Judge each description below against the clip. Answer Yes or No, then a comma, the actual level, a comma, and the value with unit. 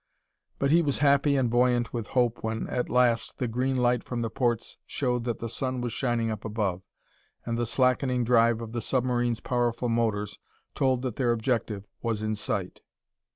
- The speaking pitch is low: Yes, low, 120 Hz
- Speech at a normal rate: Yes, average, 185 wpm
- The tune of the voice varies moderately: No, narrow, 1.8 semitones